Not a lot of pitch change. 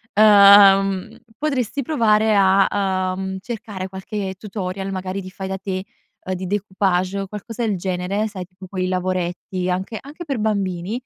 Yes: narrow, 2.1 semitones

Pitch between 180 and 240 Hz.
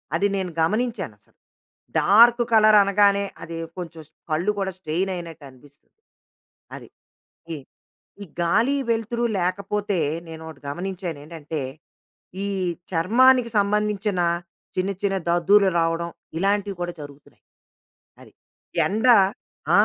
Yes: high, 190 Hz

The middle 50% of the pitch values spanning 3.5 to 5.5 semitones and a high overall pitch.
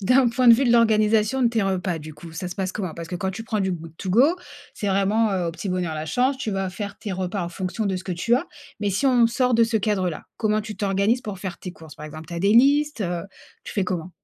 Yes: average, 4.1 semitones; high, 195 Hz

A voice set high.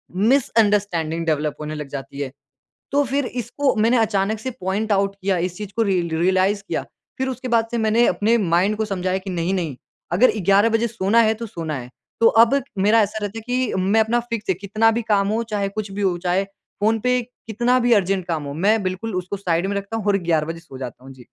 Yes: high, 200 Hz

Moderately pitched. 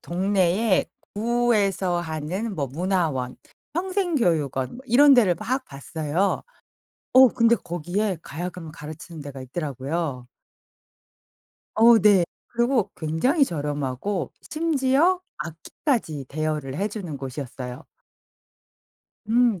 Yes: medium, 180 Hz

